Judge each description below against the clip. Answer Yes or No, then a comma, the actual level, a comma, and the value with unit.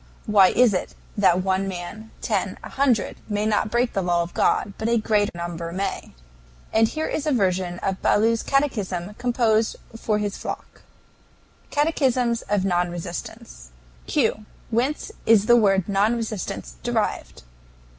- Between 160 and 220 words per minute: No, average, 150 wpm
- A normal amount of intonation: Yes, average, 4.1 semitones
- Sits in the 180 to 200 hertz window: No, high, 210 Hz